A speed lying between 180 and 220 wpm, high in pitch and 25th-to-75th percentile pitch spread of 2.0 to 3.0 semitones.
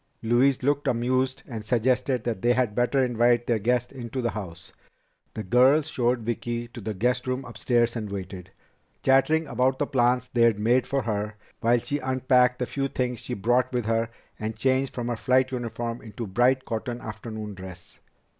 No: average, 185 wpm; low, 120 Hz; narrow, 2.4 semitones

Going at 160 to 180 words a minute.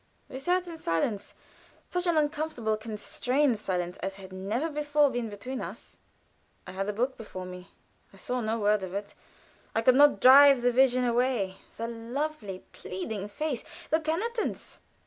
Yes: average, 165 wpm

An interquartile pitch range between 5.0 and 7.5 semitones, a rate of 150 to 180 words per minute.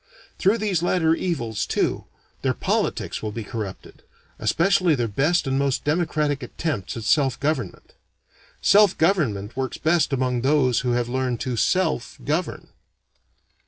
No: wide, 5.5 semitones; average, 140 wpm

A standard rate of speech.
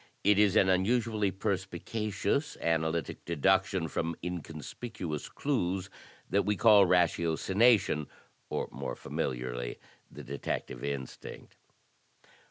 No: slow, 95 wpm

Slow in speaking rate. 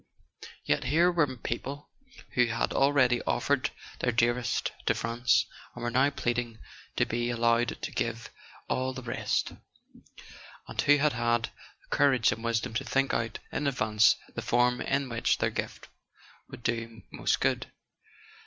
No: average, 160 wpm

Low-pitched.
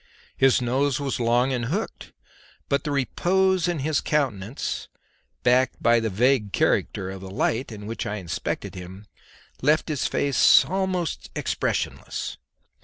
Yes: low, 130 Hz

